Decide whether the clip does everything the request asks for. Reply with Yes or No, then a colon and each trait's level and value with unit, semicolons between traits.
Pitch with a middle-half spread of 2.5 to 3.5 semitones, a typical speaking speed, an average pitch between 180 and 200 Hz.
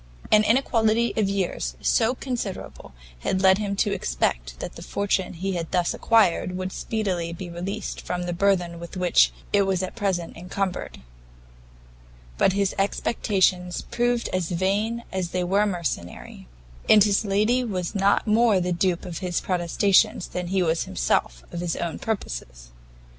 Yes: average, 2.9 semitones; average, 160 wpm; high, 190 Hz